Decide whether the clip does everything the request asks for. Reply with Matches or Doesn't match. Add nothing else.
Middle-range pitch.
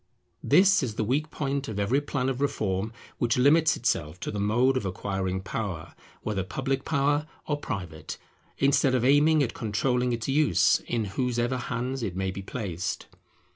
Doesn't match